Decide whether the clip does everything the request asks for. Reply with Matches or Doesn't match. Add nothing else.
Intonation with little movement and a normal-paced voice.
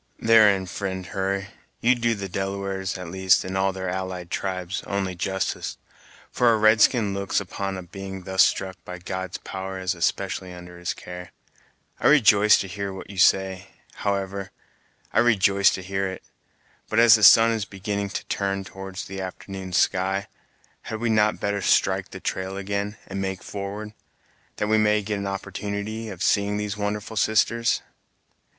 Matches